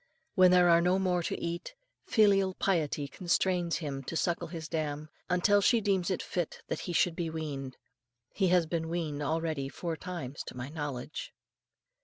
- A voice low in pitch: No, medium, 170 Hz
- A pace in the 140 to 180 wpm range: Yes, average, 175 wpm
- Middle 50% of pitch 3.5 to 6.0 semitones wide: No, average, 3.0 semitones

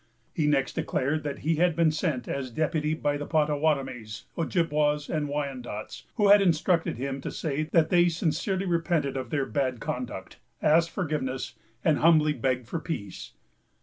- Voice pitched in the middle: Yes, medium, 150 Hz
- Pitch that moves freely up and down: No, average, 3.3 semitones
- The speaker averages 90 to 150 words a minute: No, average, 160 wpm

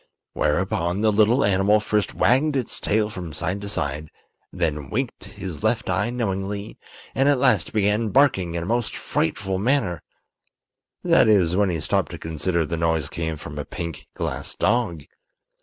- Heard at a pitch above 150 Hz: No, very low, 95 Hz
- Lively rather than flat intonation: No, average, 4.7 semitones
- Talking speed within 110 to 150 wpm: No, average, 160 wpm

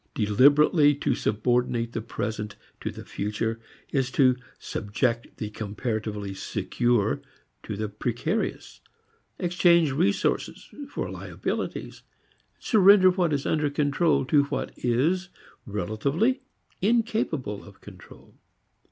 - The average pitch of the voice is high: No, low, 130 Hz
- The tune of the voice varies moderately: No, wide, 7.4 semitones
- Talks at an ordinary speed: No, slow, 105 wpm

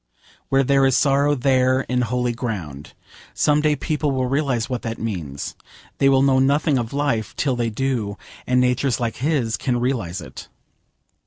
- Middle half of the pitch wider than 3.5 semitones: No, average, 3.1 semitones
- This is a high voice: No, low, 125 Hz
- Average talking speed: Yes, average, 170 wpm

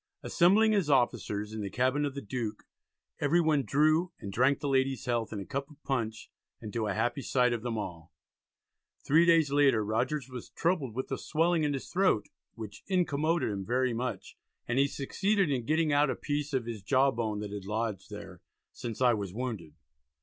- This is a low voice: Yes, low, 130 Hz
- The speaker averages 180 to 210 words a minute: Yes, average, 200 wpm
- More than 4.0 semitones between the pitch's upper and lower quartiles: Yes, average, 5.2 semitones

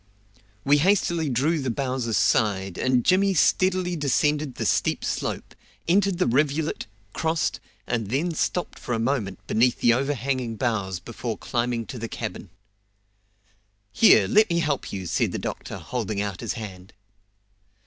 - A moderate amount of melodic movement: No, wide, 6.0 semitones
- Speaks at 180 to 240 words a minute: No, average, 150 wpm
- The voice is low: Yes, low, 130 Hz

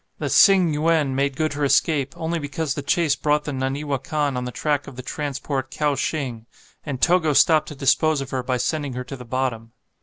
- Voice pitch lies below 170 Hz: Yes, medium, 140 Hz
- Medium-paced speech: No, fast, 210 wpm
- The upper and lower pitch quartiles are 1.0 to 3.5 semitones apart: Yes, narrow, 2.6 semitones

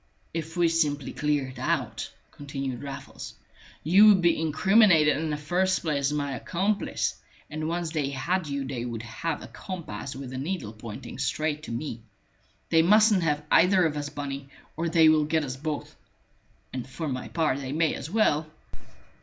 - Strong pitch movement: No, average, 3.4 semitones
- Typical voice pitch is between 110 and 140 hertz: No, medium, 150 Hz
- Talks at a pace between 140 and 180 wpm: Yes, average, 175 wpm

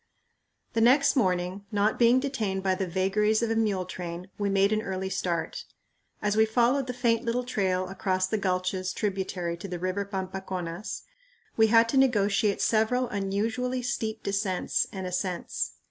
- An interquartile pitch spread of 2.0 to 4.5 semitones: Yes, average, 3.4 semitones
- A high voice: Yes, high, 200 Hz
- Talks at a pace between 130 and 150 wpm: No, average, 160 wpm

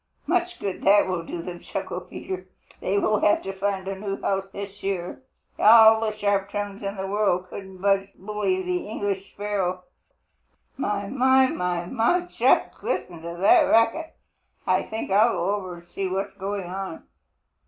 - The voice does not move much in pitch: Yes, narrow, 2.0 semitones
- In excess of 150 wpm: Yes, average, 170 wpm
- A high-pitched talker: Yes, high, 195 Hz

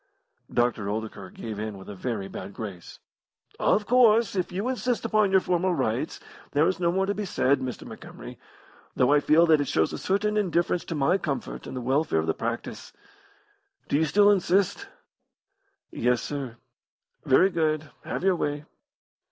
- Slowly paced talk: No, average, 175 wpm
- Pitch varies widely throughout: Yes, wide, 8.0 semitones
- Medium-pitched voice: Yes, medium, 155 Hz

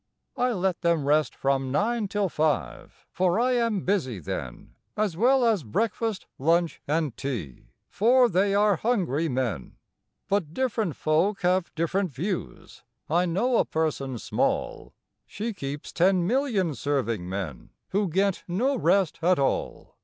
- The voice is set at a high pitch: No, medium, 180 Hz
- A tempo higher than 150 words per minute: No, average, 145 wpm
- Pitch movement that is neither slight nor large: No, wide, 6.2 semitones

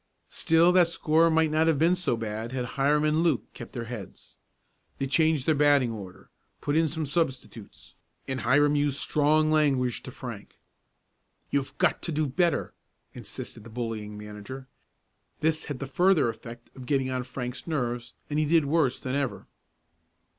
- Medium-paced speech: Yes, average, 170 wpm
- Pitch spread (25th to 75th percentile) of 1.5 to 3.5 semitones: No, average, 4.2 semitones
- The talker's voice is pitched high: No, medium, 140 Hz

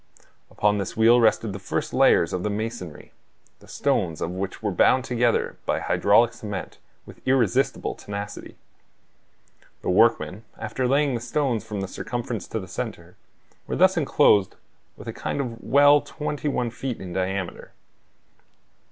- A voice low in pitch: Yes, low, 110 Hz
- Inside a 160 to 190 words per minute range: No, average, 150 wpm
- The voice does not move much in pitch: No, average, 4.2 semitones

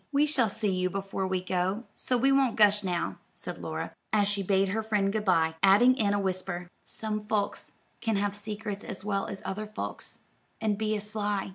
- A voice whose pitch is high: Yes, high, 205 Hz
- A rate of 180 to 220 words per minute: Yes, fast, 205 wpm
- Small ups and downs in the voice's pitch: Yes, narrow, 1.9 semitones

